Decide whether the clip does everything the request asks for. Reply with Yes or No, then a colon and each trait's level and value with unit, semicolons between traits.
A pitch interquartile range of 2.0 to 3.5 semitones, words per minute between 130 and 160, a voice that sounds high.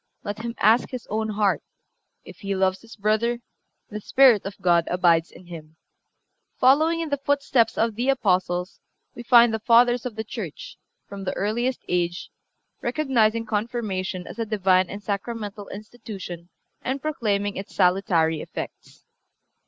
No: average, 4.1 semitones; average, 150 wpm; high, 215 Hz